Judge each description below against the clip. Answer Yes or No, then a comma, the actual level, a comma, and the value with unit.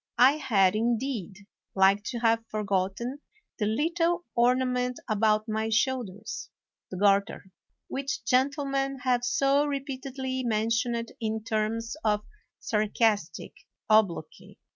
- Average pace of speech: No, slow, 110 wpm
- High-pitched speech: Yes, high, 230 Hz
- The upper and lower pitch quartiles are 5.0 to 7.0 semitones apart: No, average, 3.6 semitones